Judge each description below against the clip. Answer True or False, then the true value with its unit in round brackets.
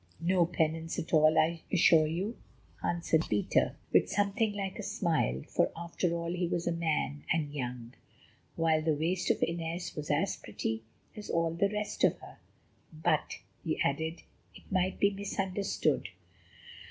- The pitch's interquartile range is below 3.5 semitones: True (2.9 semitones)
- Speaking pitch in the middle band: True (165 Hz)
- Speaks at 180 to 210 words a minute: False (155 wpm)